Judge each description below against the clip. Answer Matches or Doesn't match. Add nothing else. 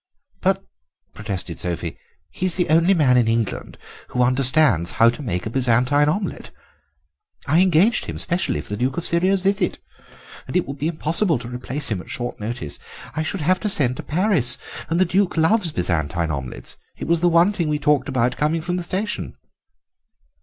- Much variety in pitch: Matches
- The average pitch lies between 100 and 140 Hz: Doesn't match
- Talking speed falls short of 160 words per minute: Doesn't match